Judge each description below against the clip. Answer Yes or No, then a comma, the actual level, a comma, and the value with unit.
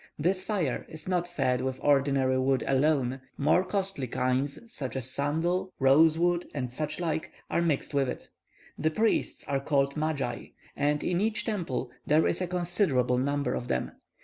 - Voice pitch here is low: No, medium, 145 Hz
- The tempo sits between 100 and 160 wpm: No, average, 170 wpm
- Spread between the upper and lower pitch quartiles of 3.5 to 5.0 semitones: Yes, average, 4.7 semitones